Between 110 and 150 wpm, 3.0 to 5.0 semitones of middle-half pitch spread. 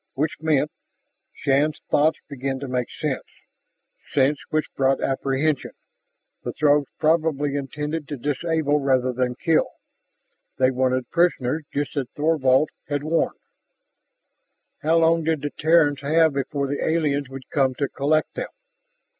No: slow, 135 wpm; narrow, 2.5 semitones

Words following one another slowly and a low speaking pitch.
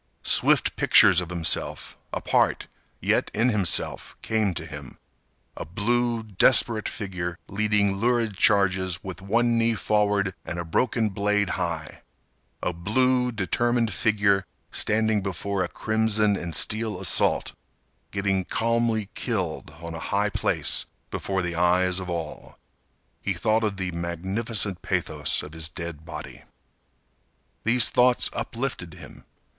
Yes: slow, 125 wpm; low, 100 Hz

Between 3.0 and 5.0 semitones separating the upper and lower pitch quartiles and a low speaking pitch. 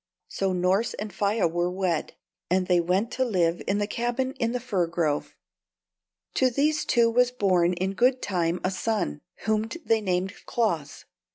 No: average, 4.6 semitones; high, 195 Hz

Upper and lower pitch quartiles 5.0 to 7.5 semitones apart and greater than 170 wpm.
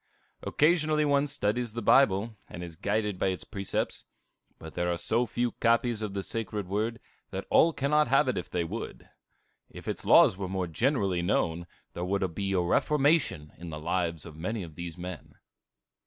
Yes: wide, 5.5 semitones; average, 185 wpm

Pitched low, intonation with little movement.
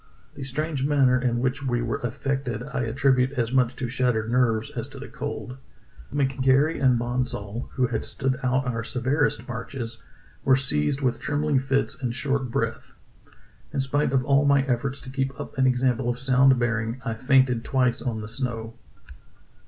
Yes: low, 130 Hz; narrow, 2.1 semitones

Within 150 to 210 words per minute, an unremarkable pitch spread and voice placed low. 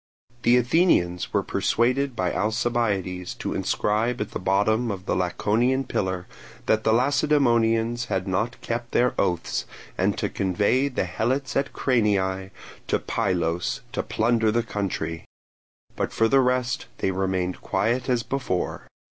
No: average, 140 wpm; average, 4.6 semitones; low, 110 Hz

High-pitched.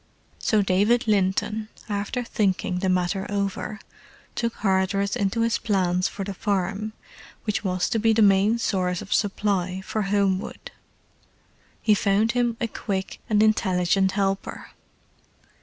Yes: high, 200 Hz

